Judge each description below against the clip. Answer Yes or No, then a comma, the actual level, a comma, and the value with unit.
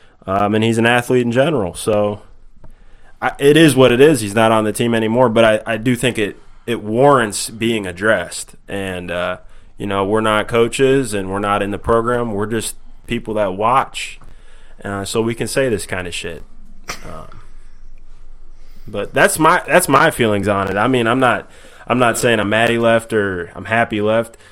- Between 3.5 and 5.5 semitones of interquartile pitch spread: No, average, 2.7 semitones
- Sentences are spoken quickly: No, average, 195 wpm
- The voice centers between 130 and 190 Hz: No, low, 110 Hz